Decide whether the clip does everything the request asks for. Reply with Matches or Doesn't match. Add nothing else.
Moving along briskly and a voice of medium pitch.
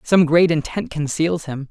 Doesn't match